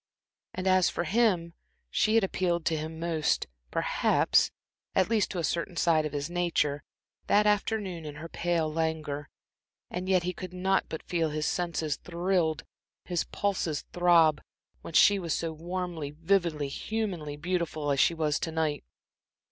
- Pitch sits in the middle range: Yes, medium, 170 Hz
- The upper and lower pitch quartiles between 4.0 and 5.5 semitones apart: No, average, 2.7 semitones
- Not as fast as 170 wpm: Yes, average, 160 wpm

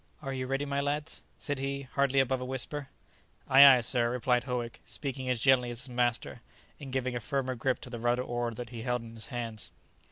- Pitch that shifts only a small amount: Yes, narrow, 2.0 semitones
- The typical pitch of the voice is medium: No, low, 125 Hz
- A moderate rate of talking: No, fast, 220 wpm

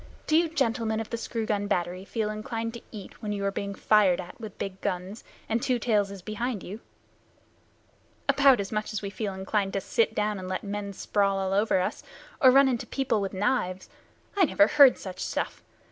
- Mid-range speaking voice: No, high, 210 Hz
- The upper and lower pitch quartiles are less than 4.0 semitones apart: Yes, average, 2.7 semitones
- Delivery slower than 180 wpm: No, fast, 205 wpm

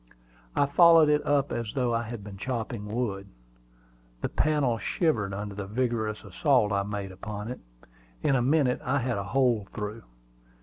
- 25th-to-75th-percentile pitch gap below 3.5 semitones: No, average, 4.5 semitones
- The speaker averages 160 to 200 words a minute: Yes, average, 170 wpm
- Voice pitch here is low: Yes, low, 115 Hz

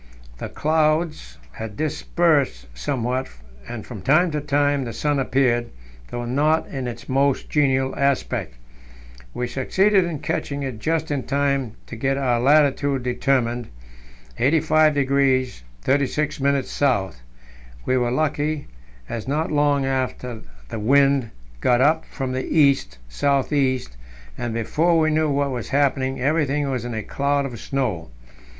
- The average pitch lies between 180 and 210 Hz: No, low, 135 Hz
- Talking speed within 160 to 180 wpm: No, average, 140 wpm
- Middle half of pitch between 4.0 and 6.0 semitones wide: No, average, 3.0 semitones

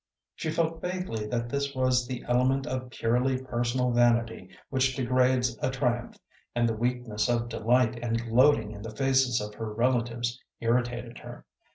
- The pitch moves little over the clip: Yes, narrow, 1.9 semitones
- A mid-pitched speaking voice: No, low, 120 Hz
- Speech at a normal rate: Yes, average, 160 wpm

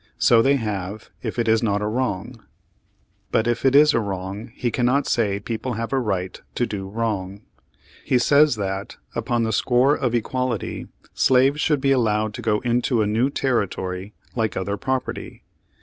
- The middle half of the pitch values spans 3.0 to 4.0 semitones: Yes, average, 3.6 semitones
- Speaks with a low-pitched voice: Yes, low, 115 Hz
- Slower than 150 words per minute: No, average, 175 wpm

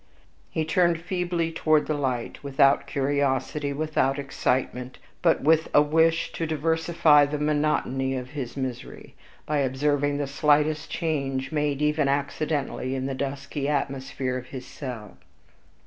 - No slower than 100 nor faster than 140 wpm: Yes, slow, 135 wpm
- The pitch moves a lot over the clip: No, narrow, 2.4 semitones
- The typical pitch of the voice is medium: Yes, medium, 145 Hz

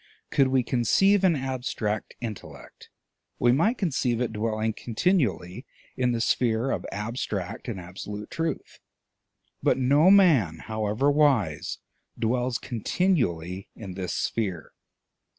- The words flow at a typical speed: No, slow, 115 wpm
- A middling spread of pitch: Yes, average, 4.5 semitones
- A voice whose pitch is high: No, low, 120 Hz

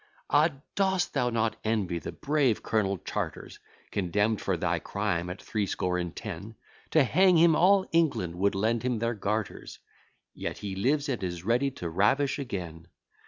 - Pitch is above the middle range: No, low, 110 Hz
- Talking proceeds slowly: No, average, 165 wpm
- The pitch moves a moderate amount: No, wide, 6.8 semitones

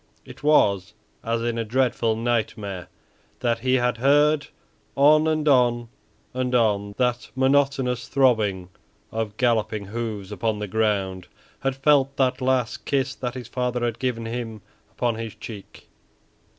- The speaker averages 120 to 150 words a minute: Yes, average, 140 wpm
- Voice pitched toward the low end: Yes, low, 120 Hz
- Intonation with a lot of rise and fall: No, average, 3.2 semitones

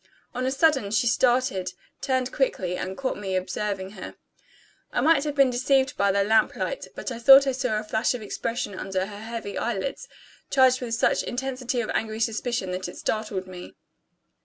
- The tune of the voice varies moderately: Yes, average, 4.5 semitones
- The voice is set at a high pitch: Yes, high, 230 Hz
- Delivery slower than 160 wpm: No, average, 185 wpm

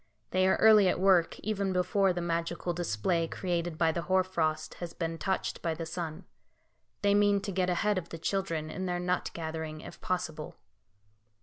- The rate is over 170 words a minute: Yes, average, 185 wpm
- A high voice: No, medium, 175 Hz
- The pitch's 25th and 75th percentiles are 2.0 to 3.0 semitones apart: Yes, narrow, 2.4 semitones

